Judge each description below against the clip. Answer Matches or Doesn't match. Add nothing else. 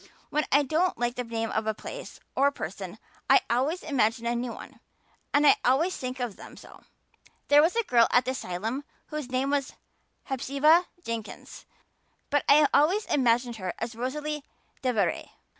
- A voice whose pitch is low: Doesn't match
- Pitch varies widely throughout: Doesn't match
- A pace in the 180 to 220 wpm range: Doesn't match